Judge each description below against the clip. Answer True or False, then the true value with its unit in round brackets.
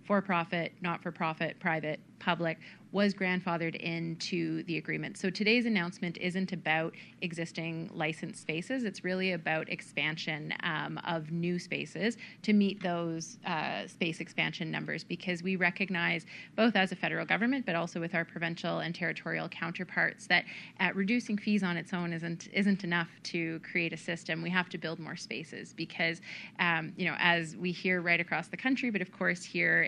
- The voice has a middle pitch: True (175 Hz)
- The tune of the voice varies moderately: False (2.3 semitones)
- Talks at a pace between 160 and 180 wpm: True (175 wpm)